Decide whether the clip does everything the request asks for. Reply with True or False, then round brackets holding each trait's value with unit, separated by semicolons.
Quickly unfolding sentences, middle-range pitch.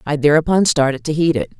True (225 wpm; 150 Hz)